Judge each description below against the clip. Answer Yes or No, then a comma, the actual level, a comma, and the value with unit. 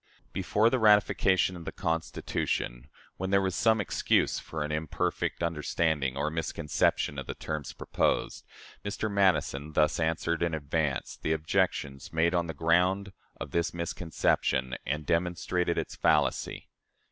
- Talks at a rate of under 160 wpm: Yes, average, 140 wpm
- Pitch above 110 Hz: No, very low, 80 Hz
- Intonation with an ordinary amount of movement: Yes, average, 3.0 semitones